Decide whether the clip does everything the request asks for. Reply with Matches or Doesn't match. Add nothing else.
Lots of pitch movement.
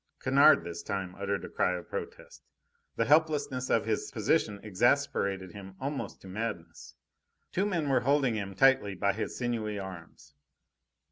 Matches